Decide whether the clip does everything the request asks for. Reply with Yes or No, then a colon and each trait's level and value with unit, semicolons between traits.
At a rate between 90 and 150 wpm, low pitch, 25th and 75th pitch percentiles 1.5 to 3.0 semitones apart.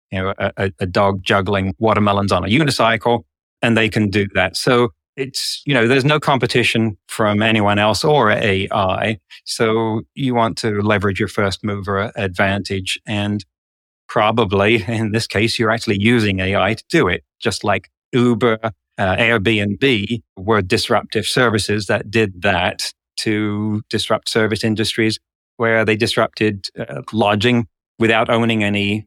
Yes: average, 145 wpm; low, 110 Hz; narrow, 2.4 semitones